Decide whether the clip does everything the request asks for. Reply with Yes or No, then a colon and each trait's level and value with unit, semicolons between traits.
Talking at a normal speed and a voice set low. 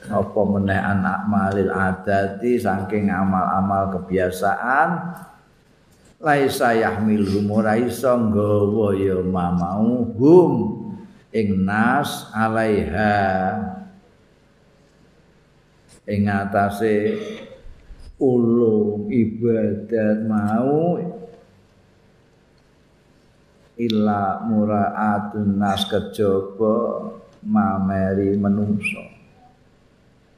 No: slow, 55 wpm; low, 105 Hz